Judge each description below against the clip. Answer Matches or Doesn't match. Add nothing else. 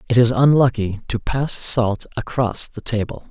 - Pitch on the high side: Doesn't match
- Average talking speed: Matches